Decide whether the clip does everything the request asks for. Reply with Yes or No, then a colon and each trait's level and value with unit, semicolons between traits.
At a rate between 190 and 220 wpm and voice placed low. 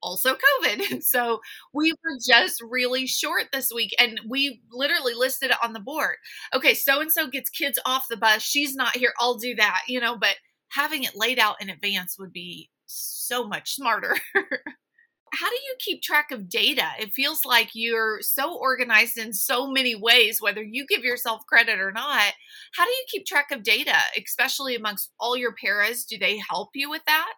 No: average, 195 wpm; high, 245 Hz